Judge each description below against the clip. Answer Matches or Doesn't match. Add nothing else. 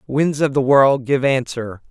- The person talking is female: Matches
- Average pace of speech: Matches